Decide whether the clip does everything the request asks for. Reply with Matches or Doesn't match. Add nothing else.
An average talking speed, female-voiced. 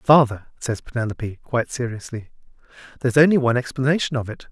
Doesn't match